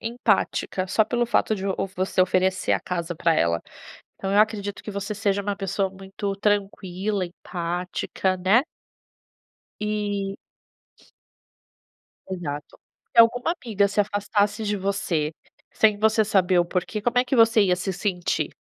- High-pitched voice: Yes, high, 200 Hz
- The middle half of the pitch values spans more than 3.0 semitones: No, narrow, 2.4 semitones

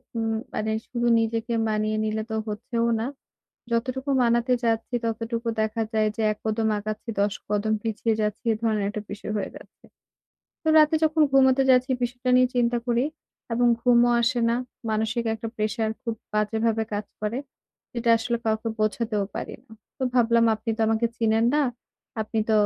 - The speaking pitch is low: No, high, 225 Hz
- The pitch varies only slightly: Yes, narrow, 1.8 semitones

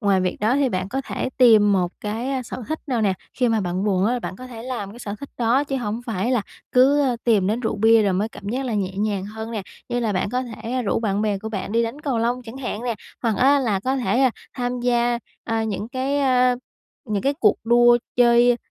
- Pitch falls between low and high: No, high, 235 Hz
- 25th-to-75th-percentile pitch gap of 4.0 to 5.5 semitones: No, average, 3.3 semitones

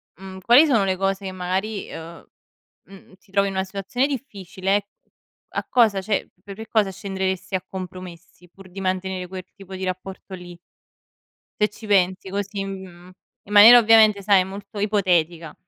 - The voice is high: Yes, high, 195 Hz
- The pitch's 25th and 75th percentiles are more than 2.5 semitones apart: No, narrow, 1.7 semitones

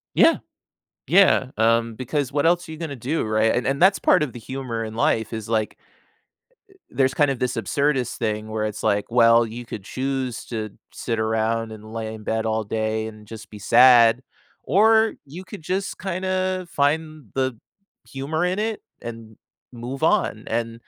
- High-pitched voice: No, low, 120 Hz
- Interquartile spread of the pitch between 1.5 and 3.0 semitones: No, average, 5.1 semitones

